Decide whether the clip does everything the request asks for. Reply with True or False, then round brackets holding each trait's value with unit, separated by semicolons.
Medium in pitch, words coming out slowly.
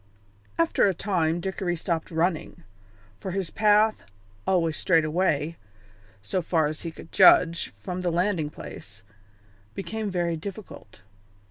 True (175 Hz; 130 wpm)